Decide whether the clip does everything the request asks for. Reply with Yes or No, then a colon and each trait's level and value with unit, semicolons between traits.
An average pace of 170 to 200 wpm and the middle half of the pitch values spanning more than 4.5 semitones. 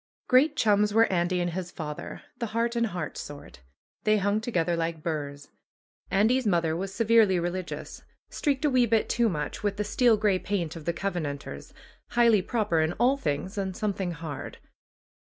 Yes: average, 175 wpm; average, 5.0 semitones